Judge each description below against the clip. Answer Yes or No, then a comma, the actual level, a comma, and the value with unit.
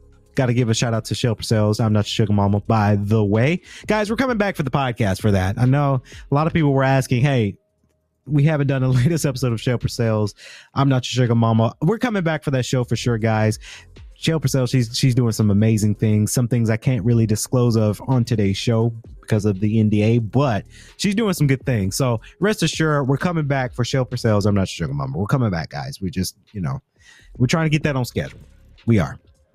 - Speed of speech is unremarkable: No, fast, 240 wpm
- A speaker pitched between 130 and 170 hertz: No, low, 120 Hz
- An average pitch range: Yes, average, 4.4 semitones